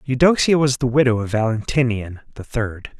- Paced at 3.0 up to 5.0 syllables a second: No, 5.2 syllables/s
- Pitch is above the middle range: No, low, 125 Hz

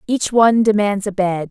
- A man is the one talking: No, female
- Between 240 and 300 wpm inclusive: No, average, 200 wpm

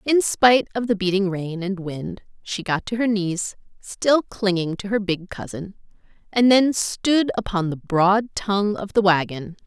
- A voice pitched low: No, high, 200 Hz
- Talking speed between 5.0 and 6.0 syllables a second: No, 4.3 syllables/s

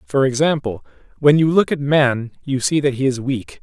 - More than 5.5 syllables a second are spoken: No, 4.9 syllables/s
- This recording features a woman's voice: No, male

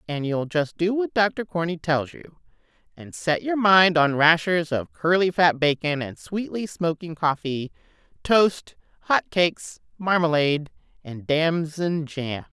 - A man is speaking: No, female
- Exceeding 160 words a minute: No, average, 145 wpm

